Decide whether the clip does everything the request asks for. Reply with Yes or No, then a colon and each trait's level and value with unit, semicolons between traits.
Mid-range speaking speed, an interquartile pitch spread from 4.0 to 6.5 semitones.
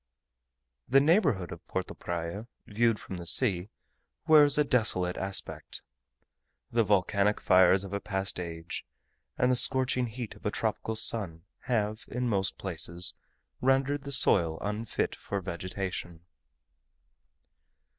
No: slow, 125 wpm; average, 5.3 semitones